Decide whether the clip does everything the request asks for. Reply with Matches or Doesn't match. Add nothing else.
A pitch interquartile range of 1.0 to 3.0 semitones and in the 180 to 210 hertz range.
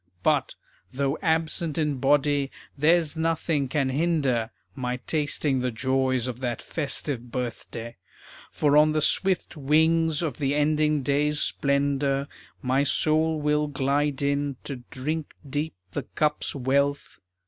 Doesn't match